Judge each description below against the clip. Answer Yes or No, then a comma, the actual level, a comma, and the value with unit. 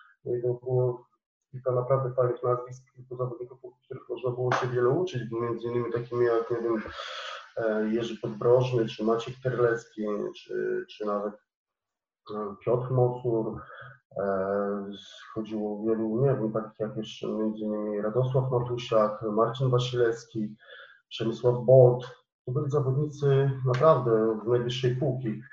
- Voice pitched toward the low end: Yes, low, 120 Hz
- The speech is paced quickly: No, average, 125 wpm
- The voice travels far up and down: No, narrow, 2.4 semitones